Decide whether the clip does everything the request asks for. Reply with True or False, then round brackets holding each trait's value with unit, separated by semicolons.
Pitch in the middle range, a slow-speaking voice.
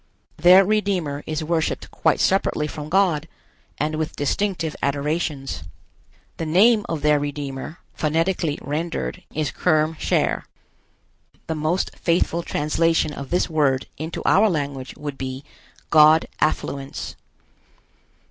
True (155 Hz; 120 wpm)